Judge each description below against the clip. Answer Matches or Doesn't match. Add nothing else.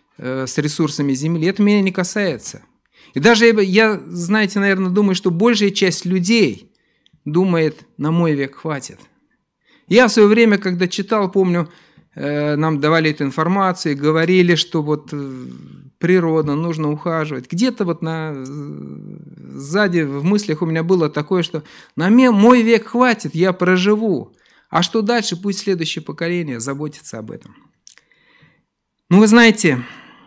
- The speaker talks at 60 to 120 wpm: Doesn't match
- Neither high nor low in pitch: Matches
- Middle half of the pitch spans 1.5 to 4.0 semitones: Doesn't match